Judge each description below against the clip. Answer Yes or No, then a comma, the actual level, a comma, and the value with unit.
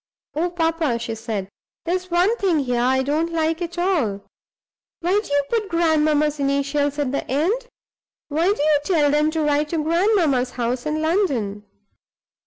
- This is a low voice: No, very high, 305 Hz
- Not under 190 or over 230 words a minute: No, average, 165 wpm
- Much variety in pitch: No, average, 3.7 semitones